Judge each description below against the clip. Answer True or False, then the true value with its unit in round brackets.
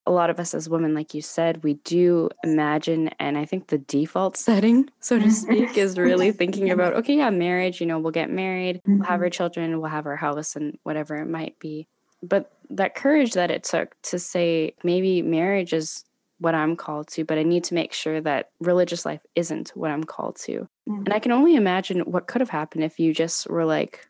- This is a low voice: False (170 Hz)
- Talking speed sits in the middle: False (220 wpm)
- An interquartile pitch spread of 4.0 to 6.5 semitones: False (3.1 semitones)